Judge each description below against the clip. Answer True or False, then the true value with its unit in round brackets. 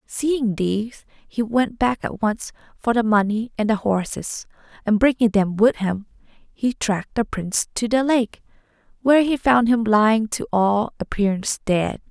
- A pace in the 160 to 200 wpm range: True (170 wpm)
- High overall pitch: True (225 Hz)